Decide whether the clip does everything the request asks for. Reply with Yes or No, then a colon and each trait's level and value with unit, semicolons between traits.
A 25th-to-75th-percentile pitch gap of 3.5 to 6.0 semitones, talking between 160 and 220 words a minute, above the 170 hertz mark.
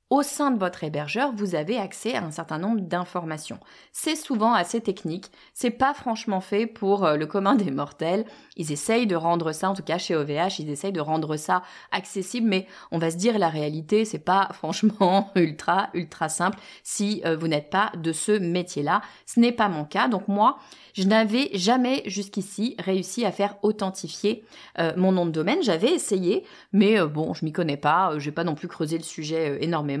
Yes: average, 4.7 semitones; average, 195 wpm; high, 190 Hz